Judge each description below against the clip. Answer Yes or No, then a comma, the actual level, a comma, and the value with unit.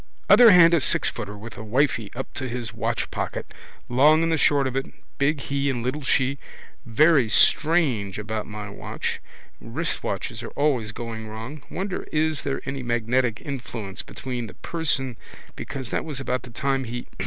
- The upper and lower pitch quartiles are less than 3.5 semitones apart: No, average, 4.1 semitones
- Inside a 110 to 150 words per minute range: No, average, 165 wpm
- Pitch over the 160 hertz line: No, low, 130 Hz